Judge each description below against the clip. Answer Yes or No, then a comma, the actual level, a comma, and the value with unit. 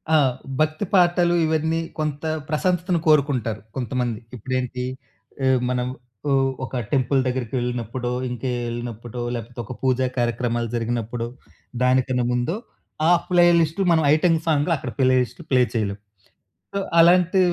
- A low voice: Yes, low, 130 Hz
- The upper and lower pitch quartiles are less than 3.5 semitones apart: No, average, 4.6 semitones